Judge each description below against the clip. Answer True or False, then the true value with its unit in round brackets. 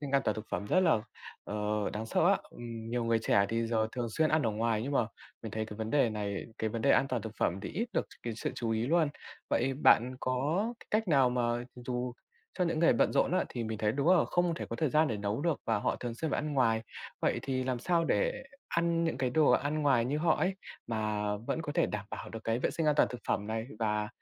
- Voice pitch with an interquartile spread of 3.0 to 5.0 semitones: False (5.4 semitones)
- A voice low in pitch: True (125 Hz)